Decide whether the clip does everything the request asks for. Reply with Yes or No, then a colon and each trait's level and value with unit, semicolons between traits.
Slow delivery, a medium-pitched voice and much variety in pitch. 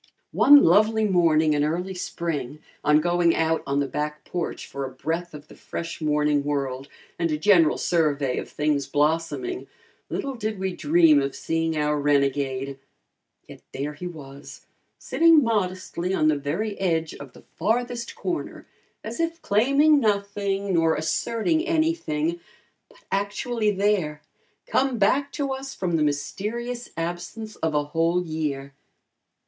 No: average, 150 wpm; medium, 170 Hz; wide, 6.1 semitones